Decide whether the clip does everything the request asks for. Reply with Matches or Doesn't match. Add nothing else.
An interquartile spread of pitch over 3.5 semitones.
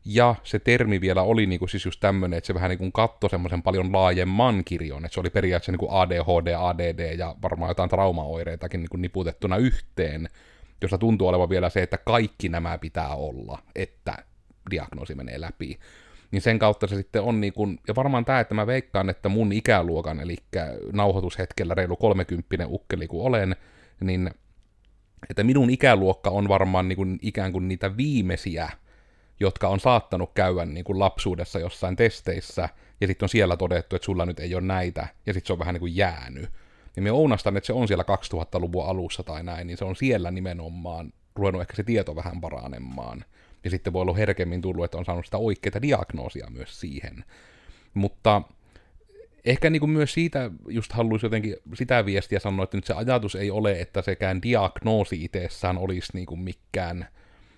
Doesn't match